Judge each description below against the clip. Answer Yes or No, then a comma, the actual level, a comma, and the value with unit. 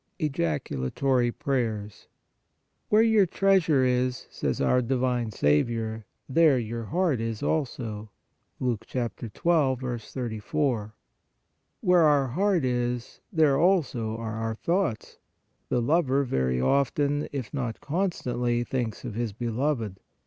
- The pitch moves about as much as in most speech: Yes, average, 4.6 semitones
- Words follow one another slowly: Yes, slow, 120 wpm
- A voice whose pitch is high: No, low, 125 Hz